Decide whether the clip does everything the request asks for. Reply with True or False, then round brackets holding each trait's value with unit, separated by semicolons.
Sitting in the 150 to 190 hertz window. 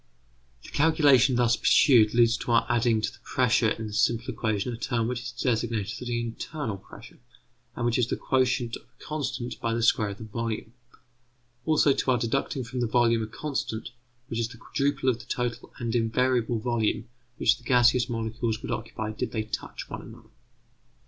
False (120 Hz)